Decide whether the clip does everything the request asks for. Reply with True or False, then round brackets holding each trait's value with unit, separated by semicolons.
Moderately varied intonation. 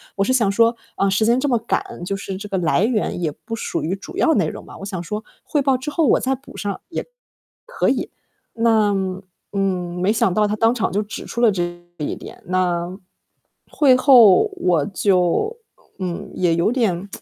True (4.5 semitones)